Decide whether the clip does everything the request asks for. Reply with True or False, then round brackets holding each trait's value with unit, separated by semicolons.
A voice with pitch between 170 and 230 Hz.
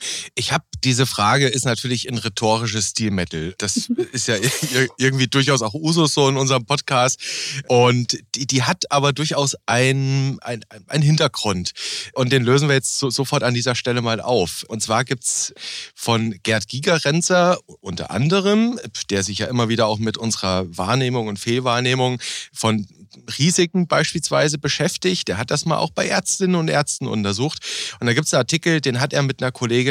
False (130 Hz)